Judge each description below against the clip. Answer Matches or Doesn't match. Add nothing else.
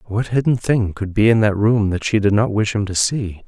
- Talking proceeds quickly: Matches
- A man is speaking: Matches